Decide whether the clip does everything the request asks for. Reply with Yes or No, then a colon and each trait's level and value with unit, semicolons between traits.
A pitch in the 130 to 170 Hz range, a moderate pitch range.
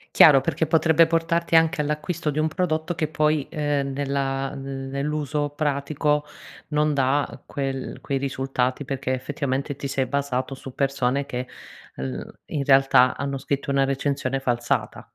No: medium, 140 Hz; narrow, 2.0 semitones